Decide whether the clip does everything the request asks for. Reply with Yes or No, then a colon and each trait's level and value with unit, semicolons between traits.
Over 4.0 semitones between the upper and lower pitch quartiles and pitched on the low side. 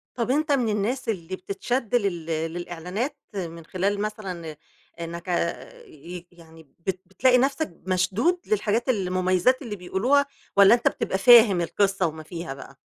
No: wide, 5.5 semitones; high, 190 Hz